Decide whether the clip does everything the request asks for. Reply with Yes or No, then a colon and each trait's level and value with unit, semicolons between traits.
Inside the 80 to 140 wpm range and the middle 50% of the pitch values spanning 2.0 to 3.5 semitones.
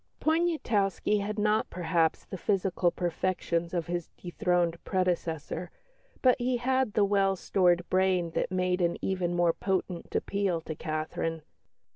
Yes: slow, 135 wpm; average, 2.8 semitones